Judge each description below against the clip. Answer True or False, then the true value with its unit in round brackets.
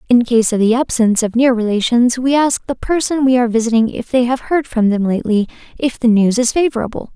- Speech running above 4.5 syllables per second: True (6.0 syllables/s)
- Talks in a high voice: True (240 Hz)